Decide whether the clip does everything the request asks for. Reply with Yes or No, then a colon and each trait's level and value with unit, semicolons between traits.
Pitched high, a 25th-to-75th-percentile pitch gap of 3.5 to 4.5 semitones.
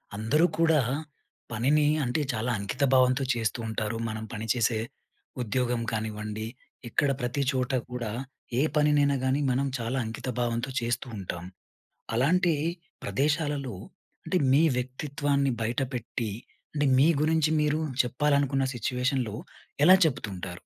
No: low, 125 Hz; average, 4.0 semitones